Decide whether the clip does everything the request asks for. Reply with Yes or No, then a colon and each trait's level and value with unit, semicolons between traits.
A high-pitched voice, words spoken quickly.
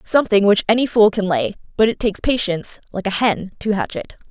Yes: high, 205 Hz; fast, 225 wpm